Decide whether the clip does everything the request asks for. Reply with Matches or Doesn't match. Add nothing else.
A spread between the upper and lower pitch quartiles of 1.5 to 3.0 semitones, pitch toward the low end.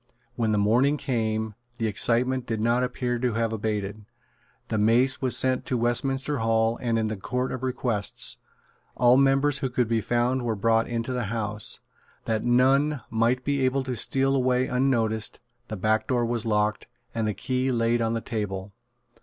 Matches